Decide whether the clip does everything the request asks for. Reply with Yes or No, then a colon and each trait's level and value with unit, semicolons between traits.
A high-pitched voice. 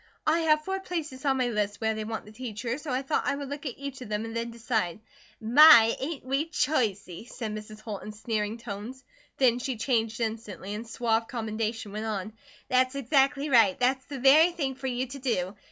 Yes: high, 240 Hz